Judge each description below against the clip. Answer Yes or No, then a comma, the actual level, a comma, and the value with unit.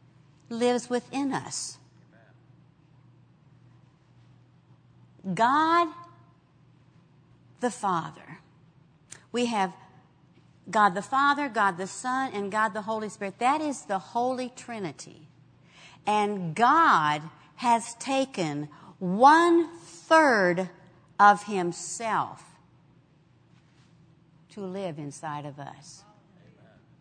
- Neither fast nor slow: No, slow, 80 wpm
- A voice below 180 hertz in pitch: No, high, 190 Hz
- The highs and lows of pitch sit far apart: Yes, wide, 7.6 semitones